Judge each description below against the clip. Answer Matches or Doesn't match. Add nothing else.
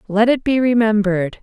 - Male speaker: Doesn't match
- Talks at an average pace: Matches